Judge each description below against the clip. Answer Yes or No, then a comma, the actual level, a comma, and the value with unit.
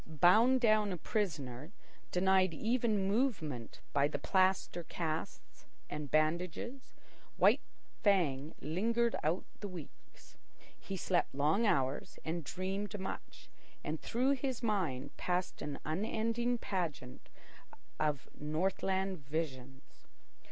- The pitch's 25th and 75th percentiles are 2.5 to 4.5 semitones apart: No, wide, 5.6 semitones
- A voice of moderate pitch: Yes, medium, 180 Hz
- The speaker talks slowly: Yes, slow, 110 wpm